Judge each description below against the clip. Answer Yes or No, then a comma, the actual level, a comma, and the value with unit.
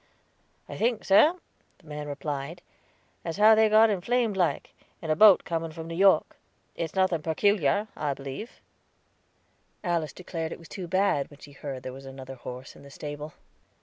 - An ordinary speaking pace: Yes, average, 175 wpm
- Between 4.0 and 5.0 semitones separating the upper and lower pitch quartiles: No, wide, 5.5 semitones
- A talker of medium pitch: Yes, medium, 165 Hz